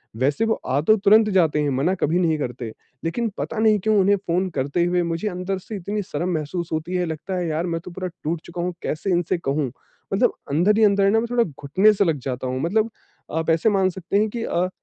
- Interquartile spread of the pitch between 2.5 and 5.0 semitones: Yes, average, 4.4 semitones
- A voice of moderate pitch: Yes, medium, 175 Hz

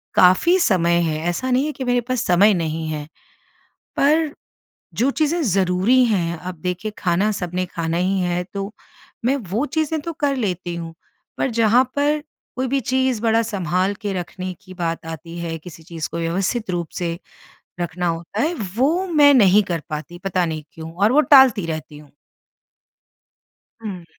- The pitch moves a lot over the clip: Yes, wide, 6.7 semitones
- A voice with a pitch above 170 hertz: Yes, medium, 185 Hz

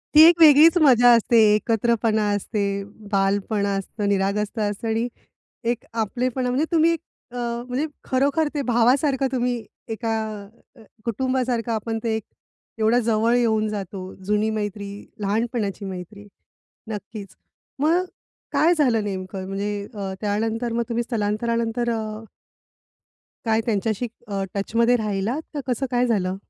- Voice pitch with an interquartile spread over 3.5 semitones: No, average, 3.1 semitones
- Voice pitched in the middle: No, high, 225 Hz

